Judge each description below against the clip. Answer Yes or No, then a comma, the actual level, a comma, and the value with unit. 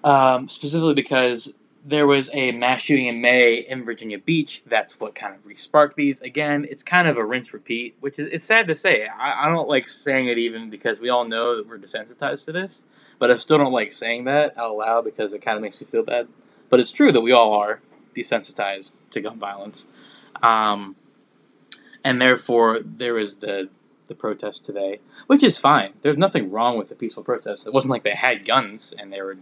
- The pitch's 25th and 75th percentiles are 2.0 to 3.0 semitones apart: No, average, 4.1 semitones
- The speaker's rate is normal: No, fast, 215 wpm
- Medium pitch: No, low, 125 Hz